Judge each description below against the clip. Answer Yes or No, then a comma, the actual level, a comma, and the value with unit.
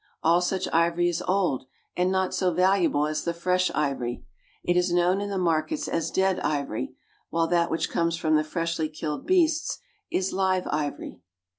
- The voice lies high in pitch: No, medium, 175 Hz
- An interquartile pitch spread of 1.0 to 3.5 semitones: Yes, average, 2.9 semitones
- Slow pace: No, average, 175 wpm